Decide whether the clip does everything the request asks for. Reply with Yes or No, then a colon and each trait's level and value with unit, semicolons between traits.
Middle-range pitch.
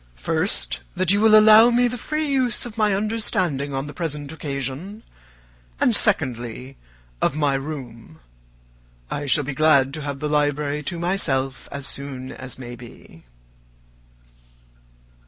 Yes: medium, 145 Hz